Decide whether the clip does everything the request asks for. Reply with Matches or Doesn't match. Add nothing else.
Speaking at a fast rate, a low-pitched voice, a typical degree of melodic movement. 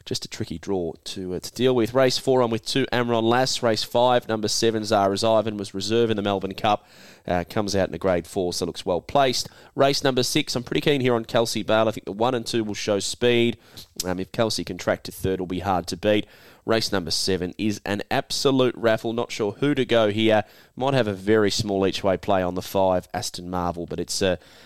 Matches